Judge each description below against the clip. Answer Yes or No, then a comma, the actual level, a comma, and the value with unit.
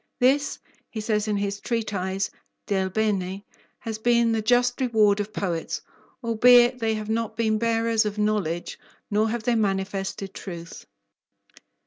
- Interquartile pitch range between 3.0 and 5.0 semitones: No, narrow, 2.6 semitones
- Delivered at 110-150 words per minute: Yes, average, 140 wpm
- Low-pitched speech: No, high, 215 Hz